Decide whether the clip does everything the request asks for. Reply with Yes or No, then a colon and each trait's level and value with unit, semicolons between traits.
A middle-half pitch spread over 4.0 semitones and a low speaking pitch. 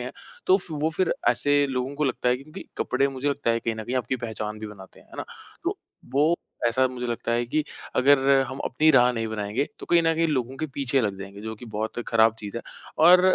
Yes: average, 4.4 semitones; low, 125 Hz